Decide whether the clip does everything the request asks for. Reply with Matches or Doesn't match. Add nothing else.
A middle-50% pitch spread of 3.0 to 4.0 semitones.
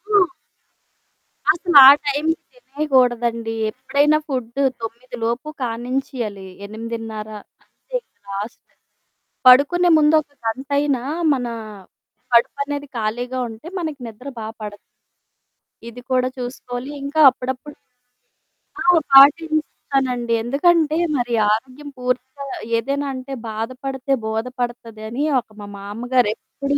Matches